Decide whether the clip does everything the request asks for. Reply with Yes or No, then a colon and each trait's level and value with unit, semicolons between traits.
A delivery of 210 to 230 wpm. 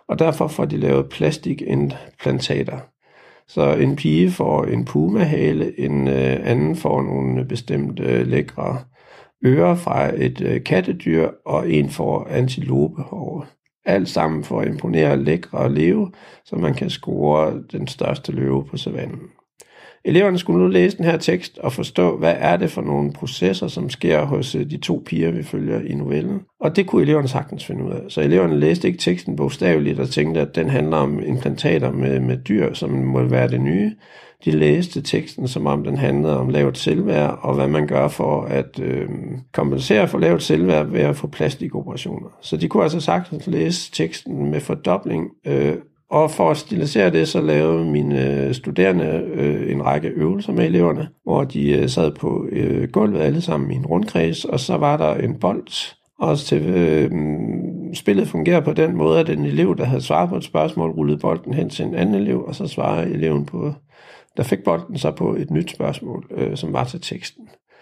No: average, 180 wpm